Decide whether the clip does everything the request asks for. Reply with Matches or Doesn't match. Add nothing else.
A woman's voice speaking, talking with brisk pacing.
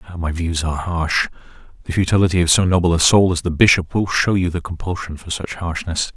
Doesn't match